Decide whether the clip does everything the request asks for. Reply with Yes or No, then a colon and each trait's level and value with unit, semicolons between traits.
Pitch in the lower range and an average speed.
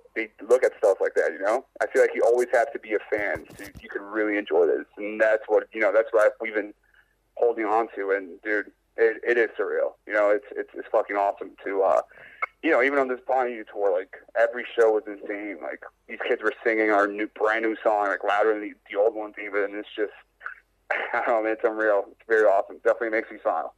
No: low, 120 Hz; fast, 240 wpm